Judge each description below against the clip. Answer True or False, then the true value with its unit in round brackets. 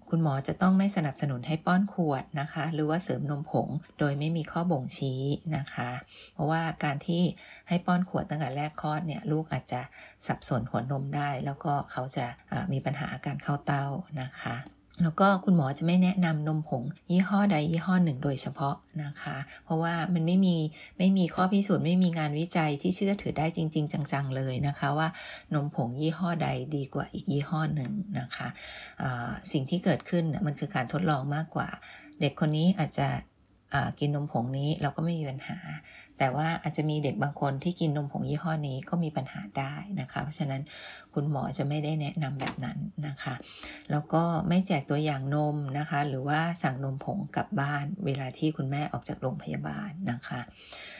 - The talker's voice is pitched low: False (155 Hz)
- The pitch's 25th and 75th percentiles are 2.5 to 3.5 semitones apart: True (3.0 semitones)